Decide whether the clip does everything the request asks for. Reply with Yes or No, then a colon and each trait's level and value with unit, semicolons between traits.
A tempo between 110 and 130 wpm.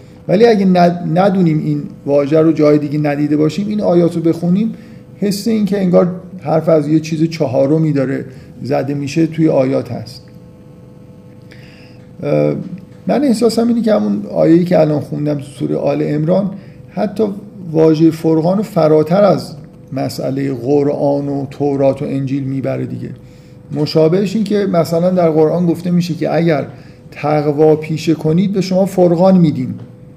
No: average, 145 wpm